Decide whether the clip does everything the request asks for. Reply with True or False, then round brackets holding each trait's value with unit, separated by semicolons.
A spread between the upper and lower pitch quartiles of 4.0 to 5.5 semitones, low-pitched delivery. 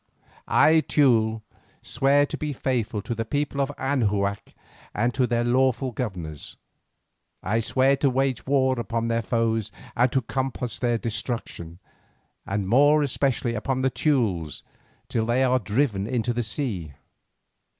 False (3.3 semitones; 120 Hz)